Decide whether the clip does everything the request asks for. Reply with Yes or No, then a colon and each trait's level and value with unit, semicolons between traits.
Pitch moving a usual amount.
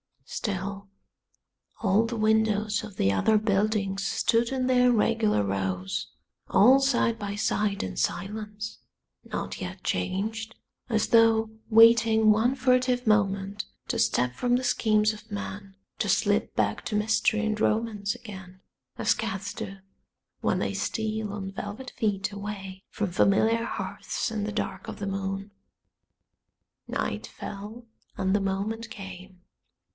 No: narrow, 2.3 semitones